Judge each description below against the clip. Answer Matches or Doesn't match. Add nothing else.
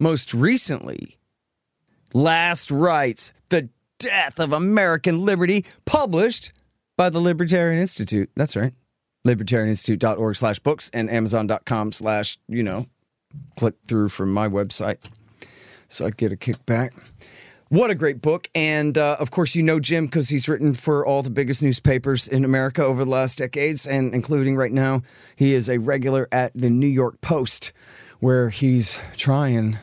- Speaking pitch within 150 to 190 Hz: Doesn't match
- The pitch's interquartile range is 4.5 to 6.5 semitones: Matches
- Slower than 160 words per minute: Matches